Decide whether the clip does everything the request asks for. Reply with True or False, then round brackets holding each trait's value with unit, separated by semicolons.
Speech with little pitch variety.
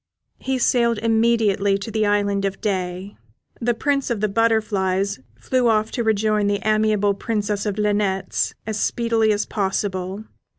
True (2.2 semitones)